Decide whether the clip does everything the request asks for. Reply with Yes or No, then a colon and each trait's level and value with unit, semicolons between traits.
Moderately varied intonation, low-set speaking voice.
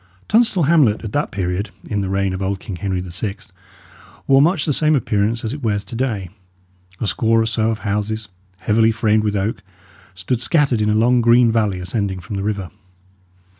Yes: average, 3.2 semitones; low, 110 Hz